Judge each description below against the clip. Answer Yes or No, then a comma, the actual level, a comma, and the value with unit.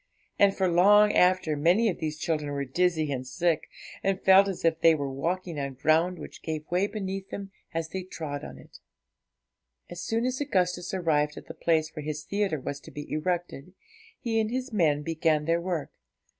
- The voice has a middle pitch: Yes, medium, 170 Hz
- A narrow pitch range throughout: No, average, 3.8 semitones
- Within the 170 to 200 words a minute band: Yes, average, 195 wpm